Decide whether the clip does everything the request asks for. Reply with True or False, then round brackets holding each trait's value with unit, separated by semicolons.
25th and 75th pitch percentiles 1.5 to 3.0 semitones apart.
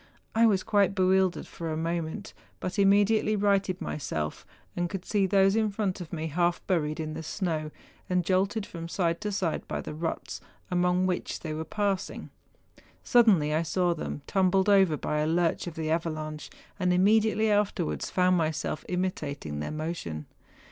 False (3.7 semitones)